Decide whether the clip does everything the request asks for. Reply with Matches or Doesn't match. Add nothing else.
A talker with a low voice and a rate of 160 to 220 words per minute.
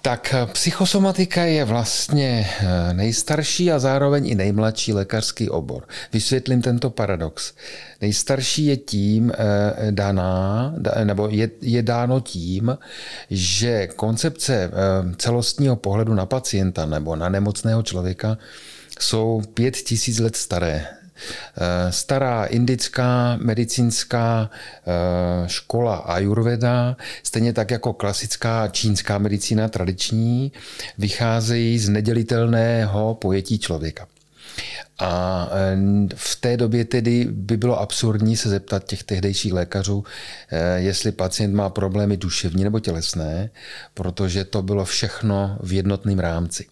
Doesn't match